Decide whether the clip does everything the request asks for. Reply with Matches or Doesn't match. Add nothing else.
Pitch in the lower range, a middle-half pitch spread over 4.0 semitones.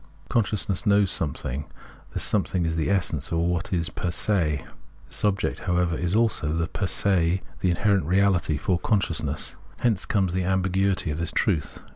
Doesn't match